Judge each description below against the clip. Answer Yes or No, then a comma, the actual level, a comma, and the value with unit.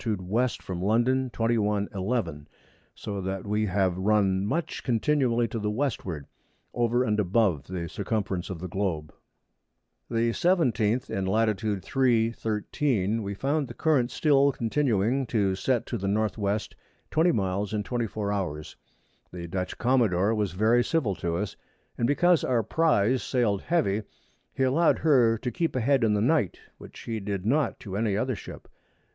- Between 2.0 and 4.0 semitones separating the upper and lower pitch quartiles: No, average, 4.4 semitones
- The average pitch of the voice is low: Yes, low, 110 Hz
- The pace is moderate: Yes, average, 160 wpm